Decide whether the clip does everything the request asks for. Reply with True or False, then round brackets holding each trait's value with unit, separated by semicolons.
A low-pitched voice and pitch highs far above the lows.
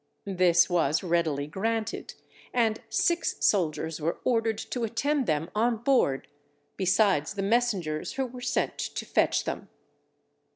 False (205 Hz; 5.8 semitones)